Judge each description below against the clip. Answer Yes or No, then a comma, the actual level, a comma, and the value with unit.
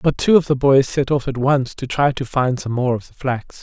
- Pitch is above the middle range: No, low, 135 Hz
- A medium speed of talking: No, fast, 300 wpm